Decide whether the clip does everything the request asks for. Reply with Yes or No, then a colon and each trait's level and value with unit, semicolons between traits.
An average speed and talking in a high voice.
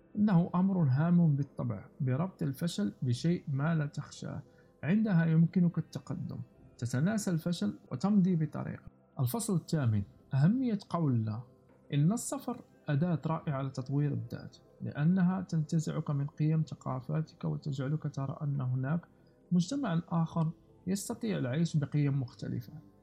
No: average, 110 wpm; medium, 155 Hz